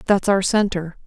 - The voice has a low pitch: No, high, 190 Hz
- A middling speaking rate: Yes, average, 170 wpm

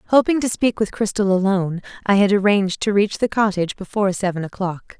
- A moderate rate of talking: Yes, average, 190 wpm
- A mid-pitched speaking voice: No, high, 200 Hz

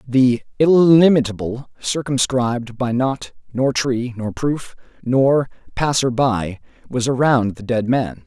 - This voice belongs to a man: Yes, male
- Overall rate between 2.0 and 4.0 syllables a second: Yes, 3.9 syllables/s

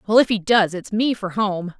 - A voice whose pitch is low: No, high, 205 Hz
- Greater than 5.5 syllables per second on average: No, 4.9 syllables/s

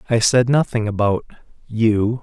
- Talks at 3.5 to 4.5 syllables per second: Yes, 4.3 syllables/s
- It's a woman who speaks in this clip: No, male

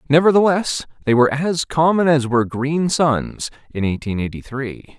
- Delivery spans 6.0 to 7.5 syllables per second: No, 4.8 syllables/s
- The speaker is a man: Yes, male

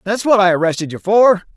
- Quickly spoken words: Yes, fast, 230 wpm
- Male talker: Yes, male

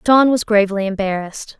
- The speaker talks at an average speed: Yes, average, 150 wpm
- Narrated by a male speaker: No, female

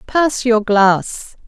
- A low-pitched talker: No, high, 235 Hz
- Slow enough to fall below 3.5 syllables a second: Yes, 2.5 syllables/s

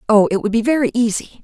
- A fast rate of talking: Yes, fast, 250 wpm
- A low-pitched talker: No, high, 225 Hz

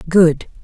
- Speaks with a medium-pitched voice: Yes, medium, 165 Hz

